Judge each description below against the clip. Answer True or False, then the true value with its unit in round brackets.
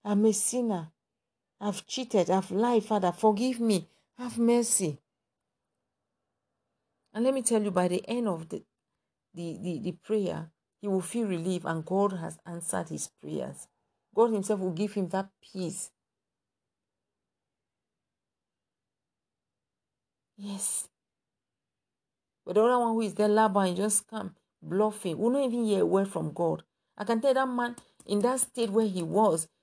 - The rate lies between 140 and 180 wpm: True (150 wpm)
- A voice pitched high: True (205 Hz)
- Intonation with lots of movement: False (4.1 semitones)